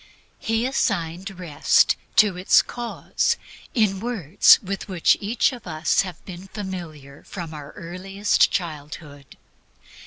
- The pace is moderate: No, slow, 120 wpm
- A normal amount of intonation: Yes, average, 4.1 semitones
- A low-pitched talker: No, medium, 185 Hz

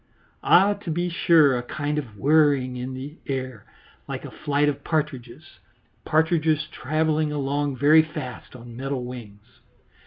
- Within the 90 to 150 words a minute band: Yes, average, 145 wpm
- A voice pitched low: No, medium, 145 Hz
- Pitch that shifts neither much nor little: Yes, average, 3.4 semitones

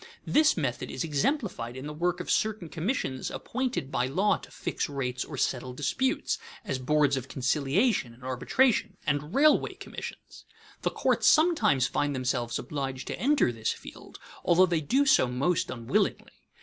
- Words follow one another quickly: No, average, 160 wpm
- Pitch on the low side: No, medium, 145 Hz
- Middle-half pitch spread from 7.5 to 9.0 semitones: Yes, wide, 8.2 semitones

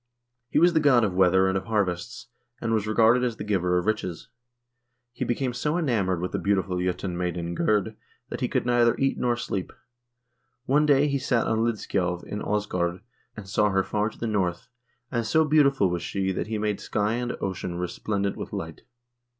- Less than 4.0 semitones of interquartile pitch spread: No, average, 4.6 semitones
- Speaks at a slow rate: No, average, 195 wpm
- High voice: No, low, 105 Hz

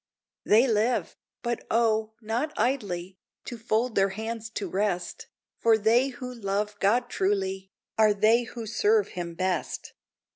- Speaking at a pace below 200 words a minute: Yes, average, 140 wpm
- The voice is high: Yes, high, 220 Hz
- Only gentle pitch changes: No, average, 3.3 semitones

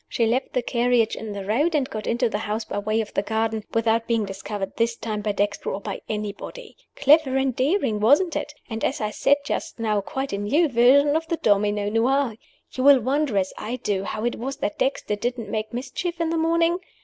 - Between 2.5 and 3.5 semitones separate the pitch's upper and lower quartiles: No, average, 4.6 semitones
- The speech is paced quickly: Yes, fast, 220 wpm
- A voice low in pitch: No, high, 230 Hz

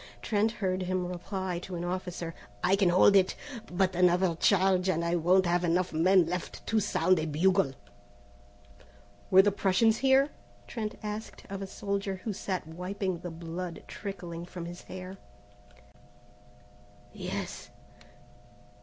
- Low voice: No, medium, 185 Hz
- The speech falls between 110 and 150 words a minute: Yes, average, 140 wpm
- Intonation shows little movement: Yes, narrow, 2.0 semitones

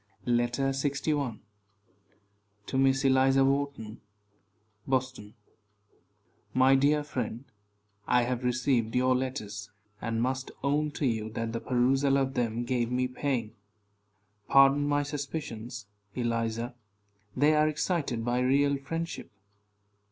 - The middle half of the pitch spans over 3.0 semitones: No, narrow, 2.6 semitones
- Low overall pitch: Yes, low, 130 Hz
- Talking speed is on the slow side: Yes, slow, 115 wpm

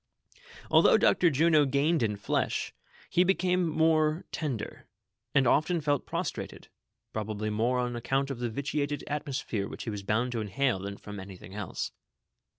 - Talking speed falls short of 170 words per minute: Yes, average, 155 wpm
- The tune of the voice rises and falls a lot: Yes, wide, 6.1 semitones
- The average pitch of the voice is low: Yes, low, 130 Hz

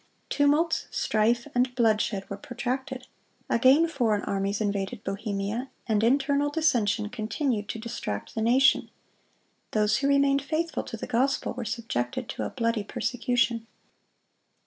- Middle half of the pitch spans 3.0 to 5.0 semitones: Yes, average, 4.0 semitones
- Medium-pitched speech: No, high, 235 Hz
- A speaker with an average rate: No, slow, 130 wpm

